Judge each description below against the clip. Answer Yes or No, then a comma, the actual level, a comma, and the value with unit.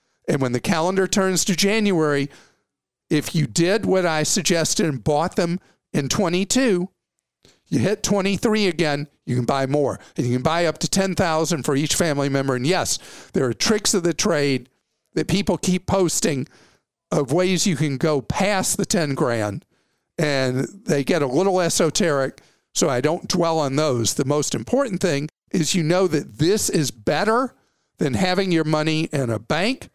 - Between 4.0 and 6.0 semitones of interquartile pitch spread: Yes, average, 4.5 semitones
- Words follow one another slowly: No, average, 175 wpm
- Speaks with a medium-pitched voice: Yes, medium, 165 Hz